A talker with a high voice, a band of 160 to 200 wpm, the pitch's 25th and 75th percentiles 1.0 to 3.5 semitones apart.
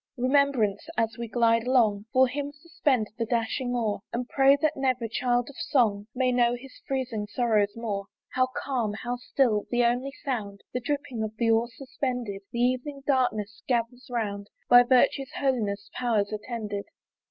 Yes: high, 245 Hz; average, 165 wpm; average, 2.9 semitones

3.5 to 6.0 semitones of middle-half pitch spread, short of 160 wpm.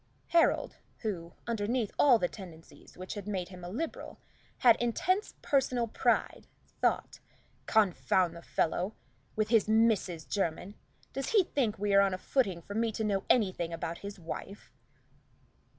Yes: average, 4.3 semitones; average, 150 wpm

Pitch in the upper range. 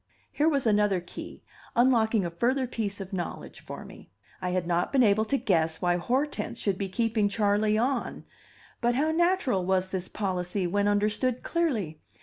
Yes: high, 210 Hz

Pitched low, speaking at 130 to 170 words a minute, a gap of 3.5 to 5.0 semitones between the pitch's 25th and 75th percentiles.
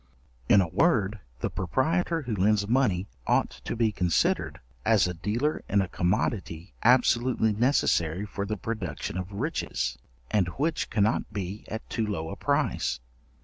Yes: low, 105 Hz; average, 150 wpm; average, 4.6 semitones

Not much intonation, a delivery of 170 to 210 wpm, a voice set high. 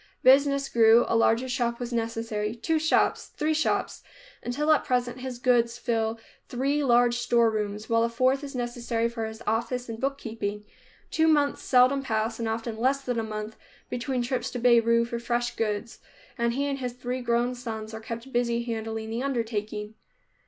Yes: narrow, 2.1 semitones; average, 175 wpm; high, 235 Hz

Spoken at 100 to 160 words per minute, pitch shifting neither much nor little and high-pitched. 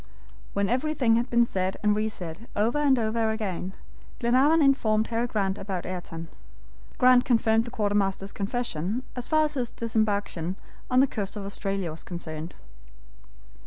Yes: average, 155 wpm; average, 3.9 semitones; high, 220 Hz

